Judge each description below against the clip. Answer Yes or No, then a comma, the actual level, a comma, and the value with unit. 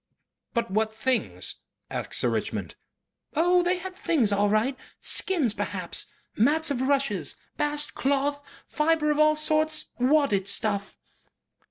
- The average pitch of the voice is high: Yes, very high, 285 Hz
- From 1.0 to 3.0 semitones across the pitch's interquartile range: No, wide, 5.6 semitones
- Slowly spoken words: Yes, slow, 130 wpm